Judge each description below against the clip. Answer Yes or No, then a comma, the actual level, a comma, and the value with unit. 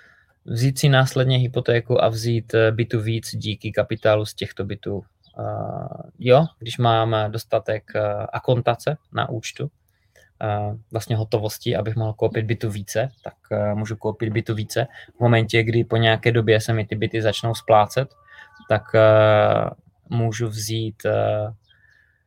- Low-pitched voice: Yes, low, 115 Hz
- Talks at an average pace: Yes, average, 125 wpm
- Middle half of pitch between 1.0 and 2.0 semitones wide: Yes, narrow, 1.6 semitones